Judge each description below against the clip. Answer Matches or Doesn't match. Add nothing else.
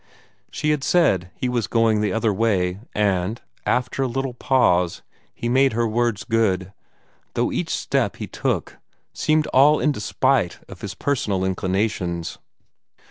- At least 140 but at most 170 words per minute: Matches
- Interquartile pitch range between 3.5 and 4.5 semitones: Doesn't match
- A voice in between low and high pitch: Doesn't match